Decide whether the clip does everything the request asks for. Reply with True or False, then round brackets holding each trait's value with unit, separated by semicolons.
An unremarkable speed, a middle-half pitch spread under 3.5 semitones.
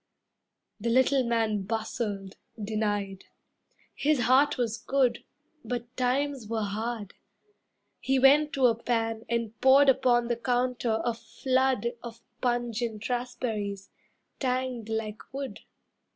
False (115 wpm; 2.6 semitones)